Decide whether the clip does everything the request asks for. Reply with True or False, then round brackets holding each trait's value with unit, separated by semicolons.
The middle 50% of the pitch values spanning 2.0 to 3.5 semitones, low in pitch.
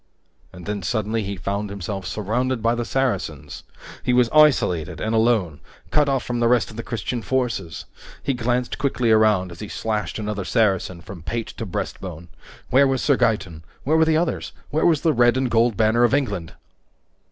False (4.2 semitones; 115 Hz)